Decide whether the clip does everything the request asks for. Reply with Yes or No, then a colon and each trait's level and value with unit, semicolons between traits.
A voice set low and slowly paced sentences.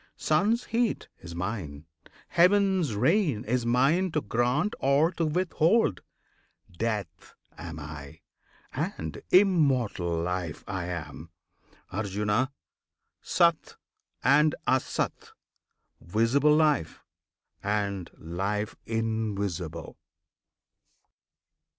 Yes: low, 115 Hz; slow, 85 wpm